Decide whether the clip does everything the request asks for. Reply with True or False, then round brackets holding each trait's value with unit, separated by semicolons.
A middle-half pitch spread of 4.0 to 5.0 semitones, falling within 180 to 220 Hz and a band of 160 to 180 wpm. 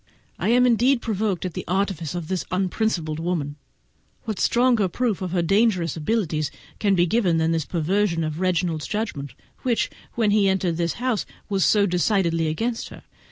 True (4.7 semitones; 185 Hz; 170 wpm)